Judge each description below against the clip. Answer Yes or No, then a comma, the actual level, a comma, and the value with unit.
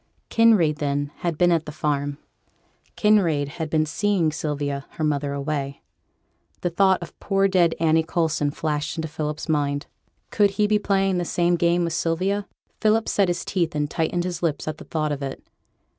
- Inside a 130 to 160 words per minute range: No, average, 180 wpm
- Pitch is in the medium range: Yes, medium, 160 Hz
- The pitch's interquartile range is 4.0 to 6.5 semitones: No, average, 3.4 semitones